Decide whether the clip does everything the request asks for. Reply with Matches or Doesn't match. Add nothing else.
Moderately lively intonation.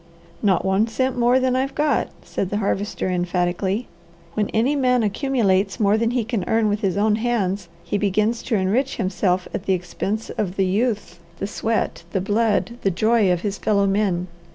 Matches